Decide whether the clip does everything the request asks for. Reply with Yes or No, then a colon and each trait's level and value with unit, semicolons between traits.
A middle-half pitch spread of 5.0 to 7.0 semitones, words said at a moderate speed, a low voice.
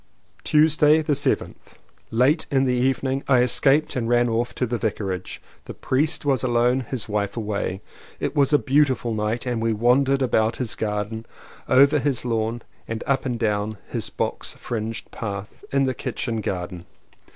No: average, 3.4 semitones; average, 165 wpm; low, 120 Hz